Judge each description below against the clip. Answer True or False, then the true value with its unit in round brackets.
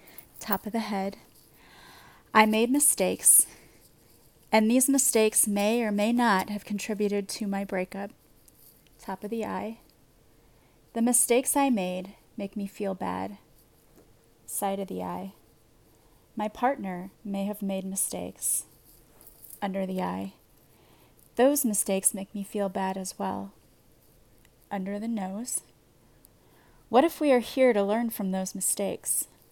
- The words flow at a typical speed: False (130 wpm)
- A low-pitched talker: False (195 Hz)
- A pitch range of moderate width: False (6.2 semitones)